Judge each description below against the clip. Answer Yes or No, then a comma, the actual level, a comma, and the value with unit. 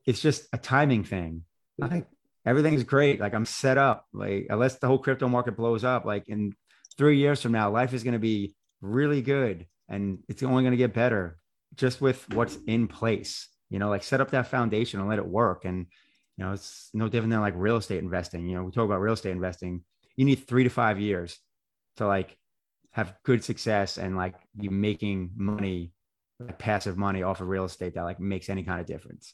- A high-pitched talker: No, low, 105 Hz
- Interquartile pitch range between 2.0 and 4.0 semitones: No, average, 4.7 semitones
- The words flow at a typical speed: No, fast, 215 wpm